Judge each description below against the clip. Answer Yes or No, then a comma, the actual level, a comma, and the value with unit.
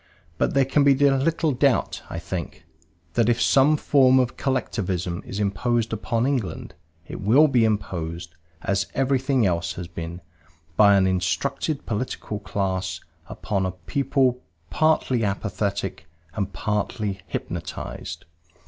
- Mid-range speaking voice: No, low, 110 Hz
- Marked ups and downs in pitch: Yes, wide, 5.9 semitones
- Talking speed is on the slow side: Yes, slow, 130 wpm